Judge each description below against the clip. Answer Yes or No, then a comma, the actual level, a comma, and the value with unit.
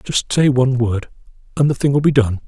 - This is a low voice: Yes, low, 130 Hz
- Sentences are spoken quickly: Yes, fast, 220 wpm